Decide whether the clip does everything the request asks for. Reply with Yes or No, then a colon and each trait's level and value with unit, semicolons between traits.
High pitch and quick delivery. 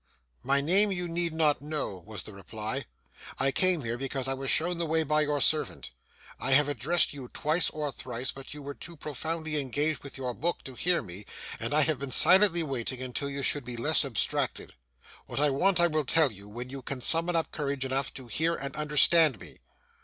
No: medium, 145 Hz; fast, 215 wpm